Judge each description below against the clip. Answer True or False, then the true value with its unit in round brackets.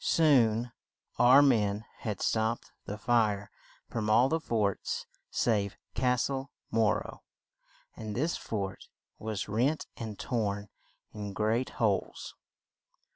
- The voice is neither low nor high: False (110 Hz)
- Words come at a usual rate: False (120 wpm)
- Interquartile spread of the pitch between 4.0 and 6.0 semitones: False (3.0 semitones)